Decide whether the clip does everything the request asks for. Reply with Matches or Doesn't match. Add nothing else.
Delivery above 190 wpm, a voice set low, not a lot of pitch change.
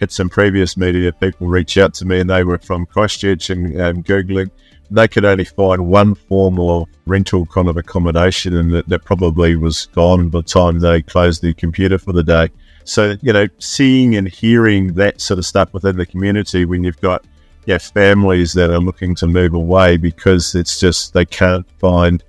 Matches